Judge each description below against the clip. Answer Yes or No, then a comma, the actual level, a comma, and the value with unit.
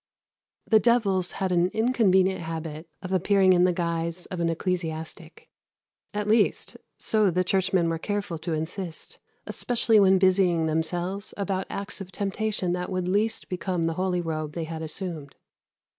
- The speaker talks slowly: No, average, 155 wpm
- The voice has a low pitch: No, medium, 185 Hz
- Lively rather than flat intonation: No, average, 2.9 semitones